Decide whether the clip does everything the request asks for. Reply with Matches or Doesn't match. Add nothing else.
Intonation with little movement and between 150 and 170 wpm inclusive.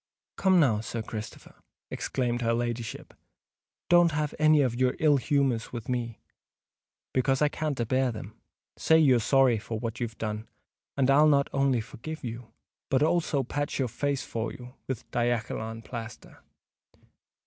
Doesn't match